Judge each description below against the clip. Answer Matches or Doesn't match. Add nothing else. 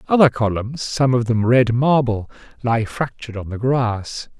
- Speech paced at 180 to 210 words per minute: Doesn't match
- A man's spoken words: Matches